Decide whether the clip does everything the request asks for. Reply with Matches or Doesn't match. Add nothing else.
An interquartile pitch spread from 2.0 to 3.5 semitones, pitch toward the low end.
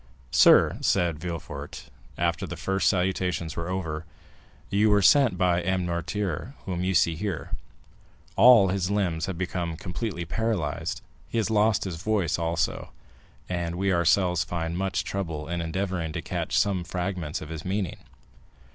Matches